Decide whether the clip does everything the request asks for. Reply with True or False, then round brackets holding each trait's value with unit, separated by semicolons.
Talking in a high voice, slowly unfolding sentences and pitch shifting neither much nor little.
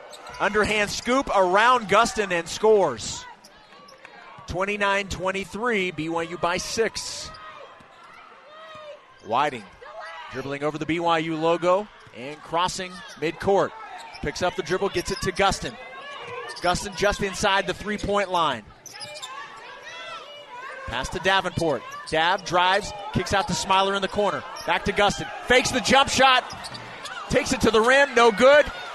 True (195 Hz; 125 wpm; 4.1 semitones)